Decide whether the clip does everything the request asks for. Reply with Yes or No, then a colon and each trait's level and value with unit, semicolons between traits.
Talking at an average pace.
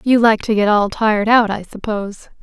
No: fast, 225 wpm